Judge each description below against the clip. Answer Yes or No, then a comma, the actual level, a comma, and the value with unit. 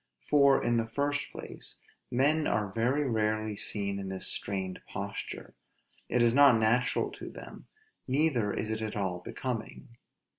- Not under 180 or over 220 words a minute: No, average, 150 wpm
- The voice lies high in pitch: No, low, 115 Hz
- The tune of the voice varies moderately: Yes, average, 4.3 semitones